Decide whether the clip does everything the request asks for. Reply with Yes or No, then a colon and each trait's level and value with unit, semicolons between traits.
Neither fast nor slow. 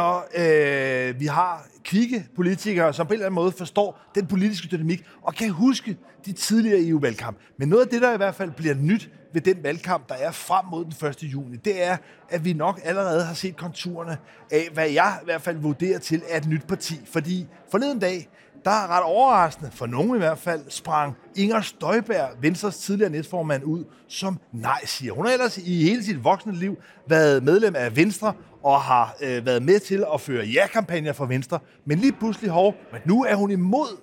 Yes: average, 205 wpm